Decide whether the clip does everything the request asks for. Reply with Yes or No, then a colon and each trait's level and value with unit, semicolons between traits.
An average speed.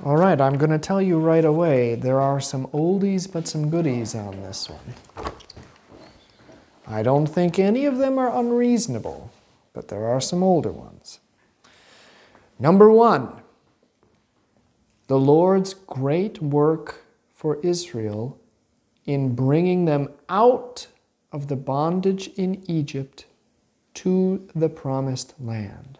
No: slow, 125 wpm